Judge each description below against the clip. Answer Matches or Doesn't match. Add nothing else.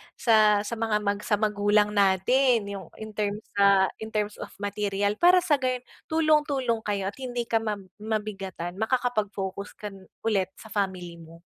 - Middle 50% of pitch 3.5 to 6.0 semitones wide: Doesn't match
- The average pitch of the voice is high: Matches